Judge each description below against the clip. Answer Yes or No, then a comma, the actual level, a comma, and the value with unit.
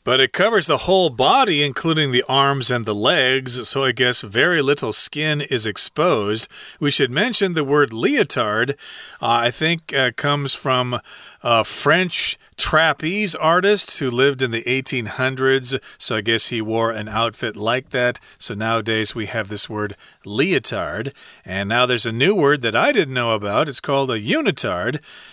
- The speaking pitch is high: No, low, 130 Hz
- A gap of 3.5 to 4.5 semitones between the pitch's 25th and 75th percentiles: Yes, average, 4.2 semitones